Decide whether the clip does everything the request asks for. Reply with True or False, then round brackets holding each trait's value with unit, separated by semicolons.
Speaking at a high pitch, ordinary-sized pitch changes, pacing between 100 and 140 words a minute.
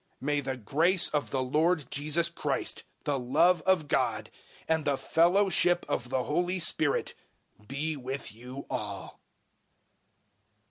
False (150 Hz; 4.3 semitones; 135 wpm)